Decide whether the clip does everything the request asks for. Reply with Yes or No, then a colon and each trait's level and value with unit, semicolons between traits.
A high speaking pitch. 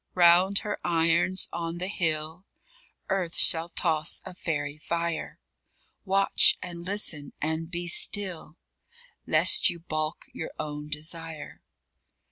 No: medium, 170 Hz